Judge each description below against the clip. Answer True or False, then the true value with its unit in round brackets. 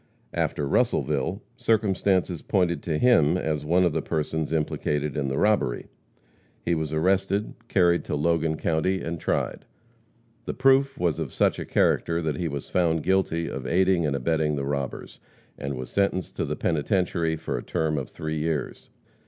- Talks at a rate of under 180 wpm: True (170 wpm)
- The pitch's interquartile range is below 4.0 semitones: True (3.5 semitones)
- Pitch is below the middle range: True (80 Hz)